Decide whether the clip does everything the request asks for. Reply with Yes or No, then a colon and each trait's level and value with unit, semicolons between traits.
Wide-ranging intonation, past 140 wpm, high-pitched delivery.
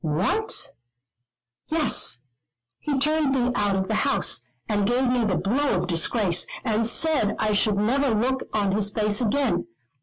No: average, 4.7 semitones; average, 155 wpm; high, 215 Hz